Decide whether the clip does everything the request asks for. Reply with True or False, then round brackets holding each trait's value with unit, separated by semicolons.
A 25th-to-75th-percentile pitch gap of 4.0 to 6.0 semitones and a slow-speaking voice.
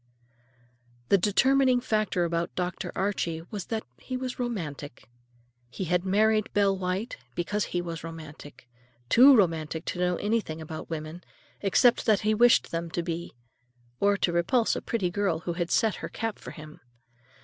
False (4.6 semitones; 160 wpm)